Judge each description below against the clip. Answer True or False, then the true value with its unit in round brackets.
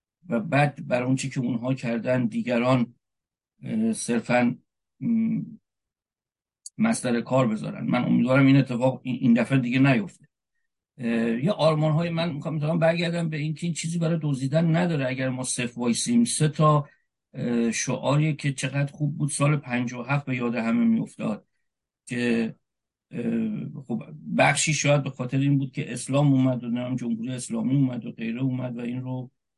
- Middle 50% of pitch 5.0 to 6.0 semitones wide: False (4.2 semitones)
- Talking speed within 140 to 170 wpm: True (150 wpm)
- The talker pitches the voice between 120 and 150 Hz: True (135 Hz)